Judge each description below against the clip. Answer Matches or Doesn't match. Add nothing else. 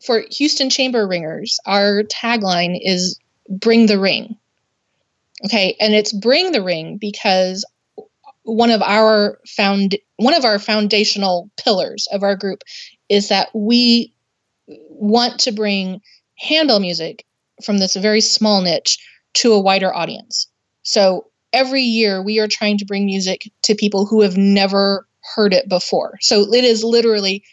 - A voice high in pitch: Matches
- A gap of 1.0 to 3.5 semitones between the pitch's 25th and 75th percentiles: Matches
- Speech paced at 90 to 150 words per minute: Matches